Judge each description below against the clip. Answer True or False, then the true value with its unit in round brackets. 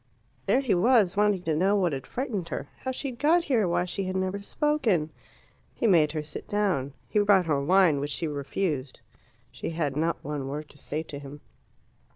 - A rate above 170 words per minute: True (200 wpm)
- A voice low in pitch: False (175 Hz)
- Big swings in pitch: True (5.7 semitones)